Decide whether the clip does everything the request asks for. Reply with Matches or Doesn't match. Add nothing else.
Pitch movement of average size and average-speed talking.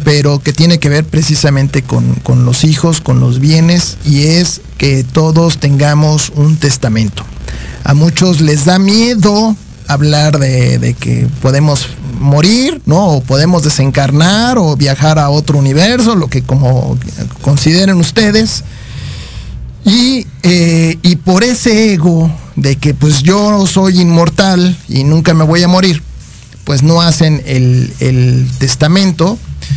Matches